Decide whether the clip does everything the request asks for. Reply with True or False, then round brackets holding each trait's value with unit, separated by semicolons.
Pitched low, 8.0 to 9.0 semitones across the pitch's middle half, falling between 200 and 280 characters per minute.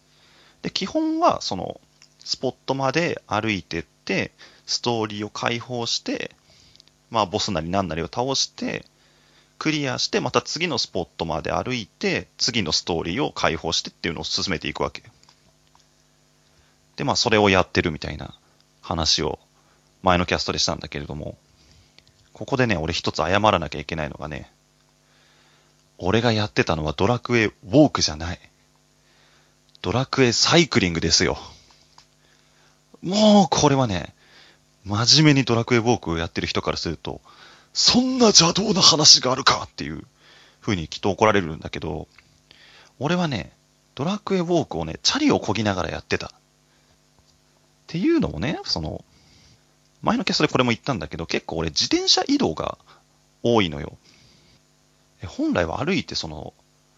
False (105 Hz; 8.5 semitones; 315 characters per minute)